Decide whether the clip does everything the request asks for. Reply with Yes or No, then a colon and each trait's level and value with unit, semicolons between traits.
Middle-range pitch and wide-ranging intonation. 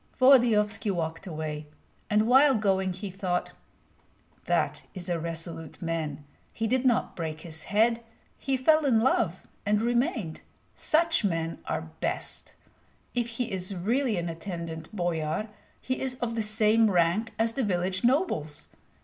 No: high, 205 Hz; wide, 6.0 semitones